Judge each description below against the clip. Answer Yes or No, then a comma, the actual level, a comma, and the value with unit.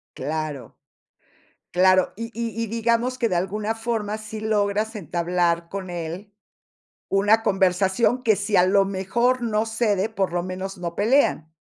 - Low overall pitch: No, high, 200 Hz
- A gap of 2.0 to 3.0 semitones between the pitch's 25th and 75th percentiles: No, average, 3.5 semitones